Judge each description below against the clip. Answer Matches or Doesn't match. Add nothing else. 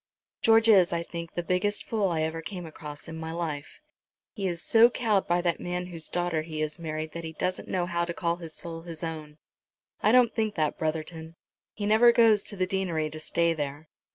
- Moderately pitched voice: Matches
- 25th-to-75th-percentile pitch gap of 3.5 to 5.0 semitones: Doesn't match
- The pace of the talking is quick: Matches